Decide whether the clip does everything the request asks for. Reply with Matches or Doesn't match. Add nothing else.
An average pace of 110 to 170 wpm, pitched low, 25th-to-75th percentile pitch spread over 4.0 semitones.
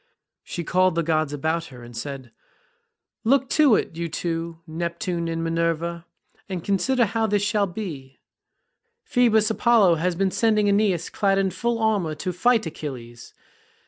Doesn't match